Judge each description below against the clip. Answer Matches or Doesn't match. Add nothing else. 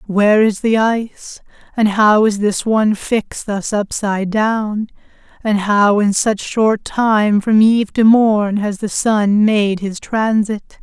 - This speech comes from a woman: Matches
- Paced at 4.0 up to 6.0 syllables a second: Doesn't match